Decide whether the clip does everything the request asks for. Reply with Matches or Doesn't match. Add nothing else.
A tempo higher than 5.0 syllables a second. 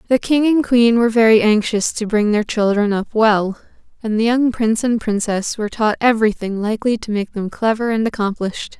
Matches